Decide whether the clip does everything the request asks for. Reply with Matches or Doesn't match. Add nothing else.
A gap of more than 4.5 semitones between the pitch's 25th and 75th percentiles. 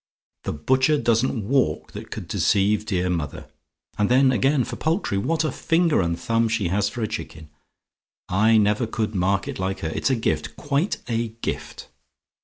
Matches